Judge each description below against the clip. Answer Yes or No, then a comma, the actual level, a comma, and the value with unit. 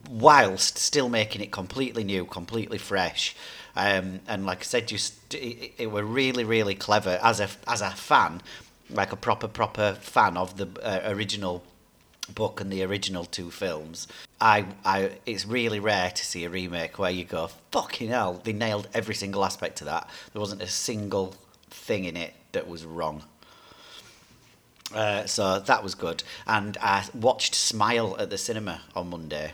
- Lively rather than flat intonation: No, average, 3.1 semitones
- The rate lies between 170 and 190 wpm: Yes, average, 175 wpm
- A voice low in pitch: Yes, low, 100 Hz